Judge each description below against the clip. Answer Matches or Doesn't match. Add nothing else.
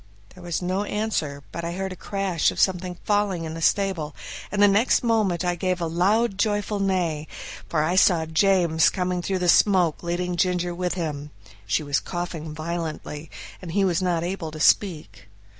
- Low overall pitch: Doesn't match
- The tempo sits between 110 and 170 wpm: Doesn't match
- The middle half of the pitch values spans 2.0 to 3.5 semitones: Matches